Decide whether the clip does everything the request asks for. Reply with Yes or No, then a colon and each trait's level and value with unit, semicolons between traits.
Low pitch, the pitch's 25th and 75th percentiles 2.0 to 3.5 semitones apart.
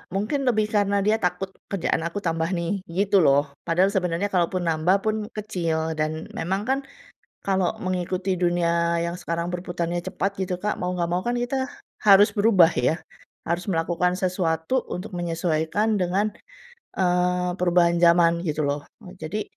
No: medium, 180 Hz; average, 2.8 semitones